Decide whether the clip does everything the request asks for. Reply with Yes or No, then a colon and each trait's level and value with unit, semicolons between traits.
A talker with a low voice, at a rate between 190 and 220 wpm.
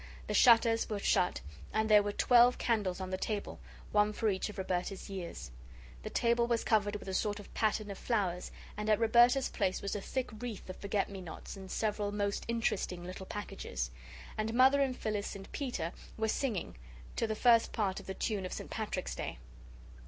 No: high, 210 Hz; average, 195 wpm